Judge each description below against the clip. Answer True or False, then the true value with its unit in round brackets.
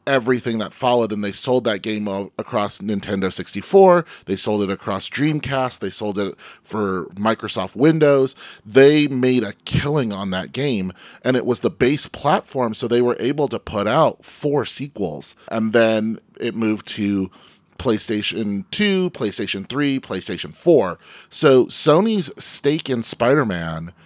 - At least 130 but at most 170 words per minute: True (150 wpm)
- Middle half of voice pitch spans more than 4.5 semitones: True (5.2 semitones)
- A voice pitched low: True (115 Hz)